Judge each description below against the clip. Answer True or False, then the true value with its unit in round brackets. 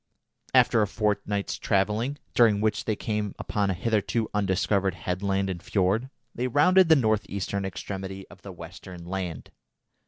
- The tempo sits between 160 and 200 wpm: False (150 wpm)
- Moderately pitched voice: False (100 Hz)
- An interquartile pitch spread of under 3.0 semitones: True (2.4 semitones)